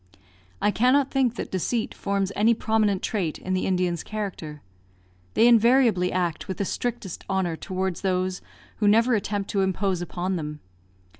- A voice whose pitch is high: Yes, high, 195 Hz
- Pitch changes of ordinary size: Yes, average, 3.3 semitones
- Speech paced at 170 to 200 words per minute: No, average, 155 wpm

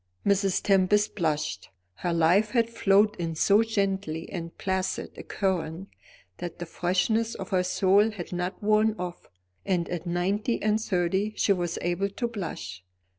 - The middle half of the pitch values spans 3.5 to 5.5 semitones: No, average, 3.0 semitones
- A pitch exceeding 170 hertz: Yes, high, 190 Hz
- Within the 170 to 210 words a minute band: No, average, 155 wpm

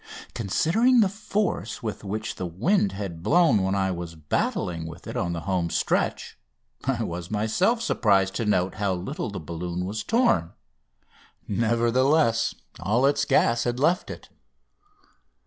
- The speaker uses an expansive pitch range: Yes, wide, 7.3 semitones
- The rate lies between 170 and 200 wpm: No, average, 145 wpm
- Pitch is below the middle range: Yes, low, 105 Hz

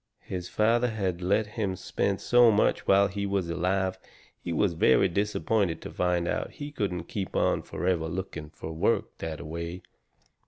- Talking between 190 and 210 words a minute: No, average, 170 wpm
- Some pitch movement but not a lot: Yes, average, 3.1 semitones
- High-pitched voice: No, very low, 95 Hz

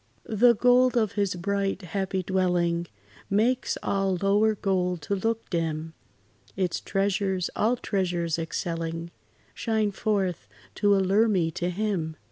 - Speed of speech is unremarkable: No, slow, 125 wpm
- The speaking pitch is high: Yes, high, 195 Hz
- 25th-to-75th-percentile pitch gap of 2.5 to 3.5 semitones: Yes, average, 3.2 semitones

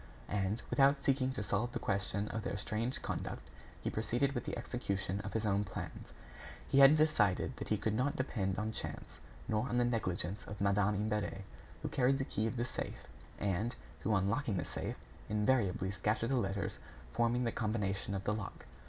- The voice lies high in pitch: No, low, 110 Hz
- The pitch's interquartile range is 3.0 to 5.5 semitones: Yes, average, 3.5 semitones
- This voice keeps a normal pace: Yes, average, 190 wpm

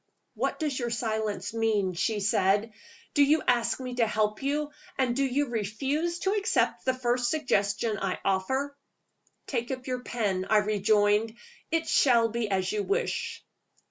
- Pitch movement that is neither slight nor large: Yes, average, 4.4 semitones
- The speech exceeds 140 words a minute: Yes, average, 160 wpm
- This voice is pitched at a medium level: No, high, 235 Hz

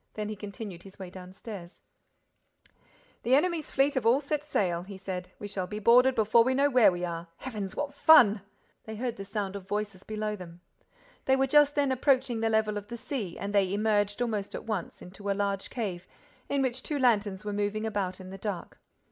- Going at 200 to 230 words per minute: Yes, fast, 205 wpm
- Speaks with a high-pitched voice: Yes, high, 210 Hz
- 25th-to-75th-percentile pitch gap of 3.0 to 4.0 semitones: No, average, 4.4 semitones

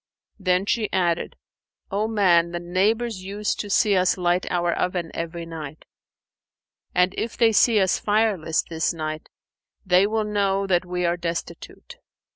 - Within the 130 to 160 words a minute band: Yes, average, 150 wpm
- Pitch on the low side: No, medium, 185 Hz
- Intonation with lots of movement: No, average, 3.2 semitones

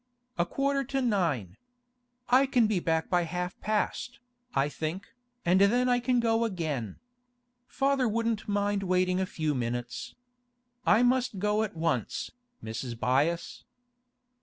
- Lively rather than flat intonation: Yes, wide, 6.5 semitones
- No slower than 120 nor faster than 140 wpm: Yes, slow, 135 wpm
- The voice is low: No, high, 190 Hz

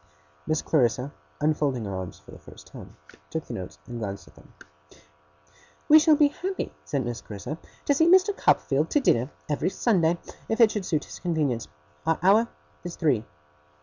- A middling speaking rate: Yes, average, 180 wpm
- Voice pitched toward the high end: No, medium, 155 Hz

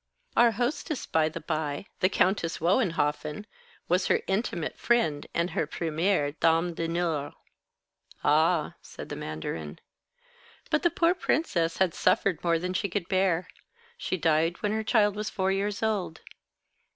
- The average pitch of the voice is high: No, medium, 175 Hz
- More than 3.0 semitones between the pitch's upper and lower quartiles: Yes, average, 4.1 semitones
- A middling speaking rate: Yes, average, 145 wpm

